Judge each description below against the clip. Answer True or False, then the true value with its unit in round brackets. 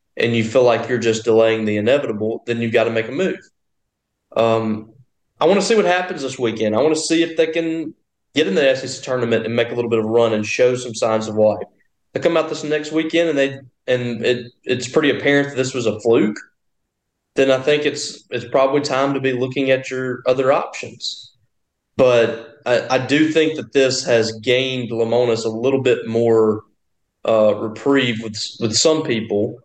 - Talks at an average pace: False (210 wpm)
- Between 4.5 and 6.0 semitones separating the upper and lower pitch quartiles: False (3.4 semitones)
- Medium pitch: False (125 Hz)